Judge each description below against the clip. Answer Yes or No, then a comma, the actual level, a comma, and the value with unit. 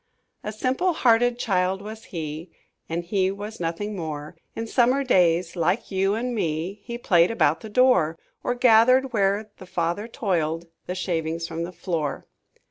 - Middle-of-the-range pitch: No, high, 195 Hz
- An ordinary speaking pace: Yes, average, 160 wpm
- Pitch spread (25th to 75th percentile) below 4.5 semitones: No, average, 5.3 semitones